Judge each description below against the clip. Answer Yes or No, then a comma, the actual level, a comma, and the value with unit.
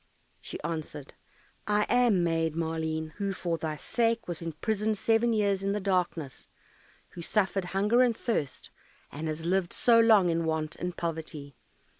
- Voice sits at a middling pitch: Yes, medium, 175 Hz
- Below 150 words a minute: No, average, 155 wpm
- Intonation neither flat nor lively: Yes, average, 4.7 semitones